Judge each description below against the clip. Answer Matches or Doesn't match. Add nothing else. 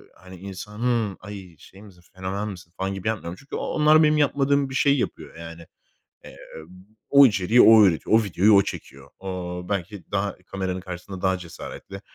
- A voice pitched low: Matches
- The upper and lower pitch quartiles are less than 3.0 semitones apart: Doesn't match